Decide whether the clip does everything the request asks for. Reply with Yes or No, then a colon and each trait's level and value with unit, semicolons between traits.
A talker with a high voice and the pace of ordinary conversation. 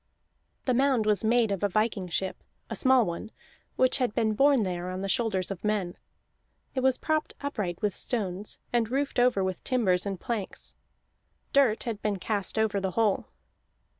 Yes: high, 215 Hz; average, 175 wpm